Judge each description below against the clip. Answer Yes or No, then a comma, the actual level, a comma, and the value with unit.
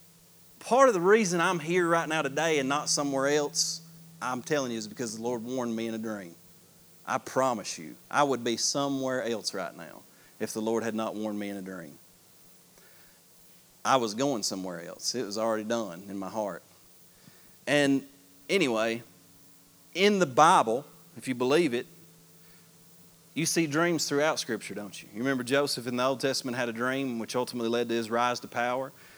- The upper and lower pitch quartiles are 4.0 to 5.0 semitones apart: Yes, average, 4.7 semitones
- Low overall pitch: Yes, low, 125 Hz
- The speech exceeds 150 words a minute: Yes, average, 185 wpm